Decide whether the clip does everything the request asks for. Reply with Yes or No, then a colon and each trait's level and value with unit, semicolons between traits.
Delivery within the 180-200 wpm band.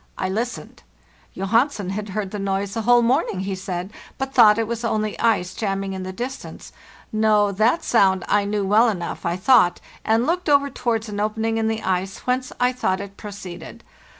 Yes: average, 190 wpm